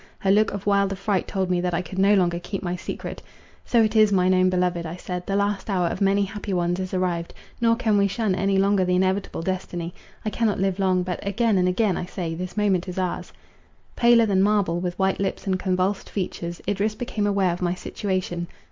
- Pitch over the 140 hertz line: Yes, high, 190 Hz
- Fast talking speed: Yes, fast, 220 wpm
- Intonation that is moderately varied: No, narrow, 1.9 semitones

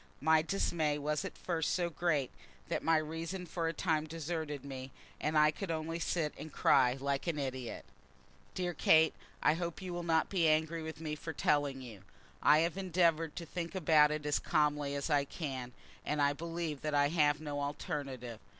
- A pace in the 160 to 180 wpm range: No, average, 190 wpm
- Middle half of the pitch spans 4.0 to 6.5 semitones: No, narrow, 2.4 semitones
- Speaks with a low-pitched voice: No, medium, 155 Hz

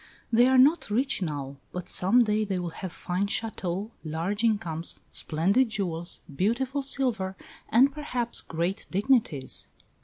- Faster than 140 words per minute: No, slow, 135 wpm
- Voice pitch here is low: No, high, 200 Hz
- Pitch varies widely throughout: Yes, wide, 5.7 semitones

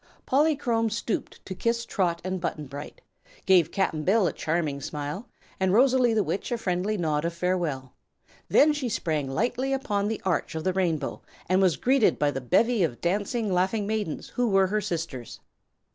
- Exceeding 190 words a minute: No, average, 175 wpm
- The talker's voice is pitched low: No, high, 190 Hz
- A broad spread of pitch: Yes, wide, 5.8 semitones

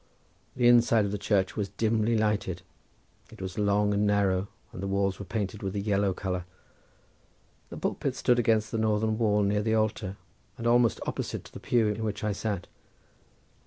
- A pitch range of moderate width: No, narrow, 2.0 semitones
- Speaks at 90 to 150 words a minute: No, average, 185 wpm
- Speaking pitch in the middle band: No, low, 105 Hz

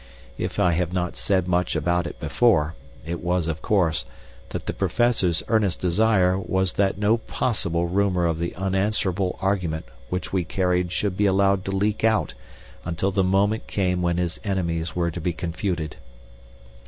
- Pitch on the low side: Yes, very low, 90 Hz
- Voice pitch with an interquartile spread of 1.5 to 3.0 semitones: Yes, narrow, 2.4 semitones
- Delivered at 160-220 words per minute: Yes, average, 165 wpm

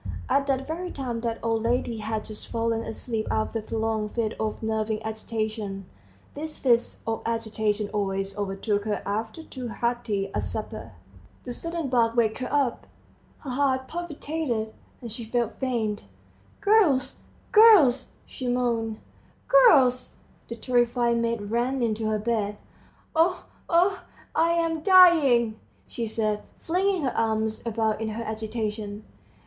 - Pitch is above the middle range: Yes, high, 230 Hz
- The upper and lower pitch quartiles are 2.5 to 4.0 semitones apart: Yes, average, 3.5 semitones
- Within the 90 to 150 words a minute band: Yes, average, 140 wpm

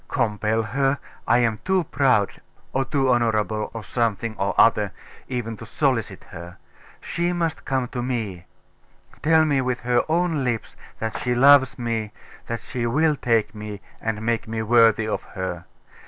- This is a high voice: No, low, 115 Hz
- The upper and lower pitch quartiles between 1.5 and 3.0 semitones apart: No, average, 3.6 semitones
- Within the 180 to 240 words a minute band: No, average, 160 wpm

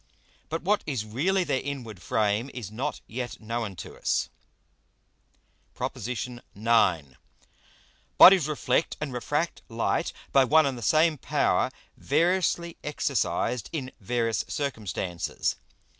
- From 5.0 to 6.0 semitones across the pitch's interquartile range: Yes, average, 5.3 semitones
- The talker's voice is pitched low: Yes, low, 130 Hz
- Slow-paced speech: Yes, slow, 115 wpm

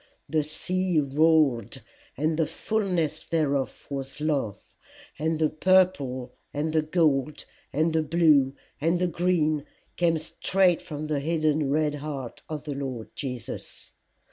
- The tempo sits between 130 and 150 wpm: Yes, slow, 135 wpm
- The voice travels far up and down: No, average, 2.7 semitones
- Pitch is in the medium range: Yes, medium, 155 Hz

